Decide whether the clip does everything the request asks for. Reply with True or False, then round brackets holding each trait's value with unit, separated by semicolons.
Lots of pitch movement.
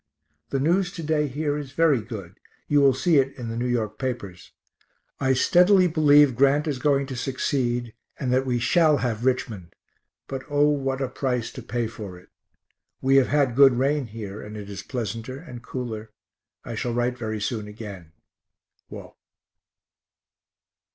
False (4.0 semitones)